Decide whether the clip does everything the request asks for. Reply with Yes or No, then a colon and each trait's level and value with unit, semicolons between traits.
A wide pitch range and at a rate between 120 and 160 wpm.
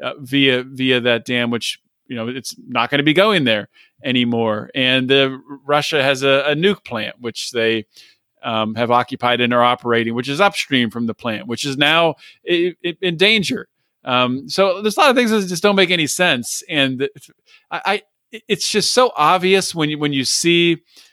No: wide, 6.7 semitones; average, 195 wpm